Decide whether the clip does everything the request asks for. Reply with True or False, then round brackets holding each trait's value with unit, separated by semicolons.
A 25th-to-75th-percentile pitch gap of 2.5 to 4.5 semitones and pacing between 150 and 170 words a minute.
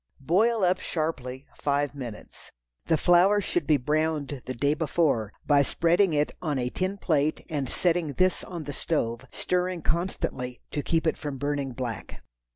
True (4.1 semitones; 160 wpm)